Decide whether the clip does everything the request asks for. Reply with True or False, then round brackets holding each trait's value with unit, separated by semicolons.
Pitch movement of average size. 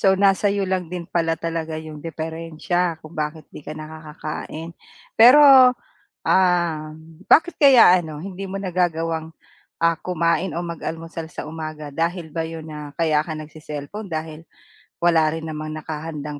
False (2.2 semitones)